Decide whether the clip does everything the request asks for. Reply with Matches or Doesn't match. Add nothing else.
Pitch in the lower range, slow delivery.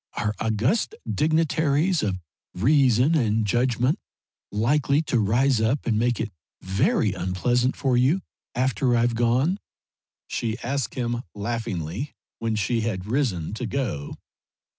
Matches